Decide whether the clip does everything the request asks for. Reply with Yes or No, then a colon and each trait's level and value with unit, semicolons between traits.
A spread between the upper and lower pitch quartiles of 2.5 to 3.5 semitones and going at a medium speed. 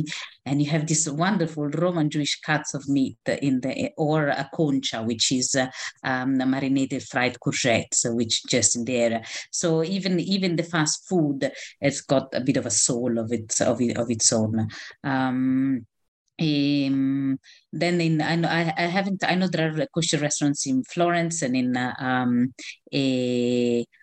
No: average, 4.1 semitones; average, 170 wpm